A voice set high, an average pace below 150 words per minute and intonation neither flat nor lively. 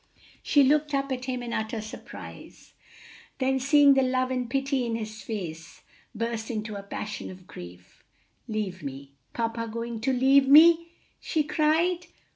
No: high, 245 Hz; average, 155 wpm; average, 4.2 semitones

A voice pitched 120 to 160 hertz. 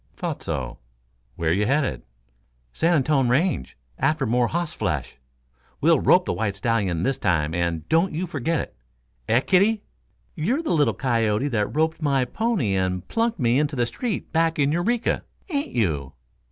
Yes: low, 135 Hz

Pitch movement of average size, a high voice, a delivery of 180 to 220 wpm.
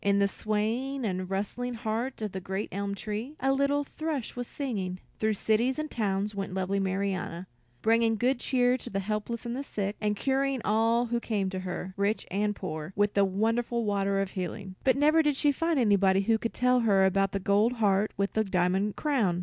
Yes: average, 3.9 semitones; high, 210 Hz; average, 200 wpm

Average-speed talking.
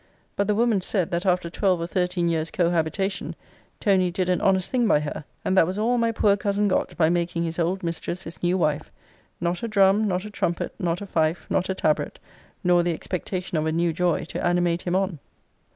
No: fast, 215 wpm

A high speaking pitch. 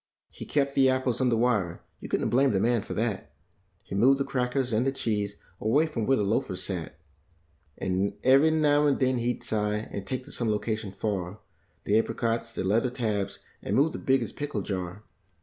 No: low, 115 Hz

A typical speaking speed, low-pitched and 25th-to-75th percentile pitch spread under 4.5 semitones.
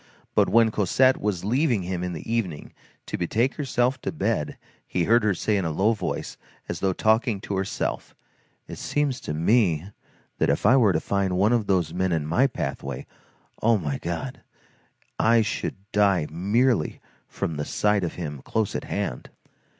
No: average, 180 wpm; low, 100 Hz; average, 4.9 semitones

